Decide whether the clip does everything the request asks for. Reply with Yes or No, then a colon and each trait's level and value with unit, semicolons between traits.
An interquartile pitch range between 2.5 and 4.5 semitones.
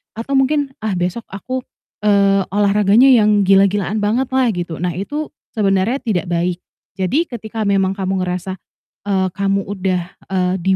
Yes: average, 2.8 semitones